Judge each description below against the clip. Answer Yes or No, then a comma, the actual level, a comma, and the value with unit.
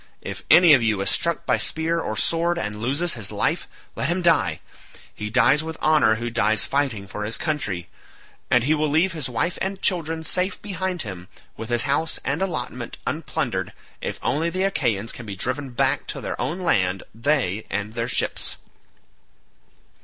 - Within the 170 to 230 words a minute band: Yes, average, 180 wpm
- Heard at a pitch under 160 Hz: Yes, low, 135 Hz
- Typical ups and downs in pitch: No, wide, 7.0 semitones